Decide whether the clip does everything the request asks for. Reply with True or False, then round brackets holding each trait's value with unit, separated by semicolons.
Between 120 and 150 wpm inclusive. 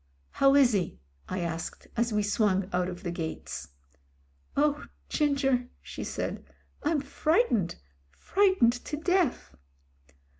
True (140 wpm)